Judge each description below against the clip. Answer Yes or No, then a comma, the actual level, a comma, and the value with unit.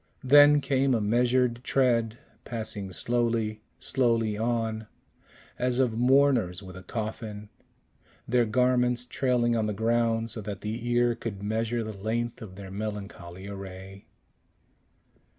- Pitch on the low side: Yes, low, 115 Hz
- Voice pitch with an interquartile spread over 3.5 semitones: No, average, 2.7 semitones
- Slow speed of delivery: Yes, slow, 130 wpm